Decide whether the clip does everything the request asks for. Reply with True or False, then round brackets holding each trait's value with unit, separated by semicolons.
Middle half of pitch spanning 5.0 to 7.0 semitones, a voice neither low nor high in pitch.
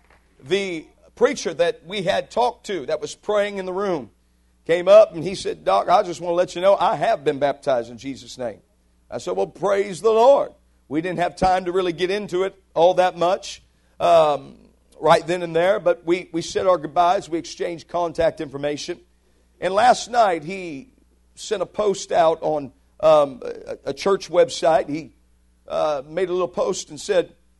True (5.4 semitones; 175 Hz)